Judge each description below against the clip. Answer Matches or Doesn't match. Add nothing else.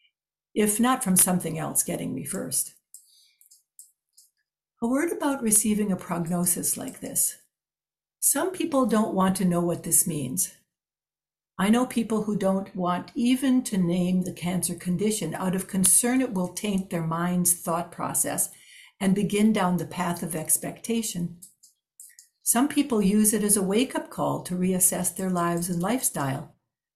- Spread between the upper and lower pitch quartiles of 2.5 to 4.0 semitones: Doesn't match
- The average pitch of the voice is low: Doesn't match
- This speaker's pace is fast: Doesn't match